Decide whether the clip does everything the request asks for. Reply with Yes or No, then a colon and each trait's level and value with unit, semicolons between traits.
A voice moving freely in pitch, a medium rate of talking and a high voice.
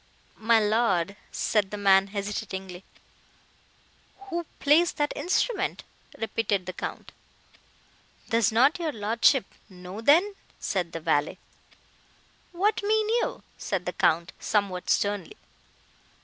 No: wide, 8.3 semitones; slow, 110 wpm; high, 215 Hz